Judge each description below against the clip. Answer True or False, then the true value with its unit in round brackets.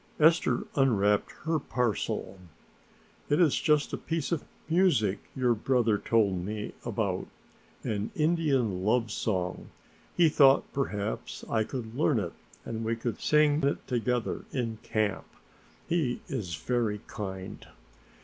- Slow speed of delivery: True (130 wpm)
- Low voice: True (120 Hz)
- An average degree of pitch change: False (5.7 semitones)